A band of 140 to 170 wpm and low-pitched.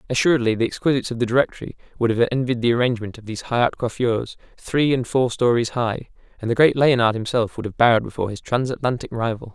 No: fast, 205 wpm; low, 120 Hz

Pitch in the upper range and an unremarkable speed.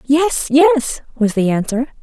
Yes: very high, 270 Hz; average, 150 wpm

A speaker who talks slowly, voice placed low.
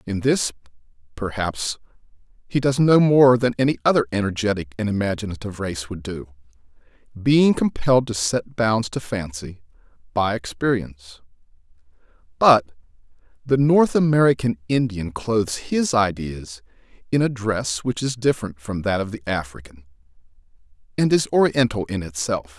Yes: slow, 130 wpm; low, 110 Hz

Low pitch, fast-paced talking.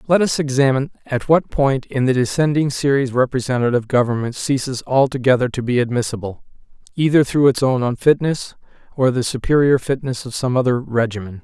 No: low, 130 Hz; average, 155 wpm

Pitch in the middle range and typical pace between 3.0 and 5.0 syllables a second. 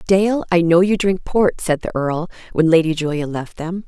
Yes: medium, 175 Hz; 4.7 syllables/s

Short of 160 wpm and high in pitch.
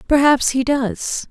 Yes: average, 140 wpm; very high, 270 Hz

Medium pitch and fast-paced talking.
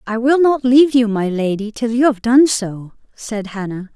No: high, 230 Hz; fast, 210 wpm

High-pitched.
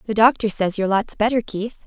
Yes: high, 215 Hz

